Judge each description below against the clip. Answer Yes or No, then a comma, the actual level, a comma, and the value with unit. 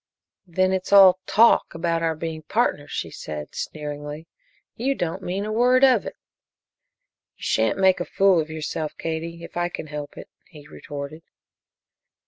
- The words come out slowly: No, average, 160 wpm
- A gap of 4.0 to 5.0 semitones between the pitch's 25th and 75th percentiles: No, average, 3.6 semitones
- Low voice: No, medium, 165 Hz